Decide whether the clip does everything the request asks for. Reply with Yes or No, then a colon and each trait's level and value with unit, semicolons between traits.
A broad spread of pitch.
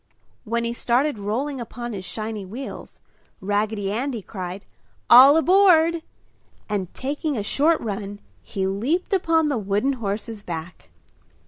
Yes: wide, 5.8 semitones